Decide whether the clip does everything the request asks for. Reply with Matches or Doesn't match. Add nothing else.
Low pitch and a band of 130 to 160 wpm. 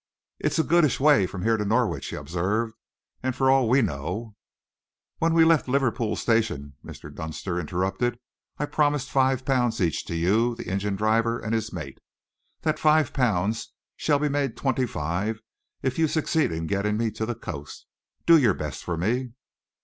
Doesn't match